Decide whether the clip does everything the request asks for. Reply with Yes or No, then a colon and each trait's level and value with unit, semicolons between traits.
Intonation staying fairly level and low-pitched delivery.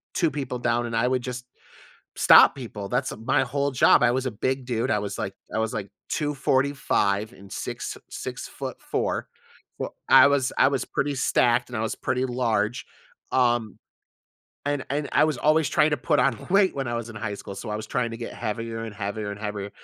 No: average, 3.6 semitones; low, 120 Hz